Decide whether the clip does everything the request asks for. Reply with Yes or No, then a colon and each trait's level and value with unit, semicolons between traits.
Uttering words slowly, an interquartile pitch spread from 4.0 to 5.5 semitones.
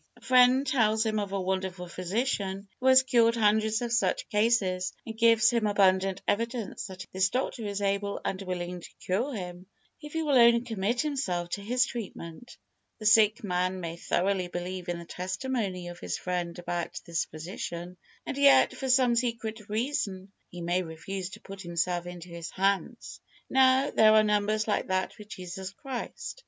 No: average, 175 wpm; average, 4.3 semitones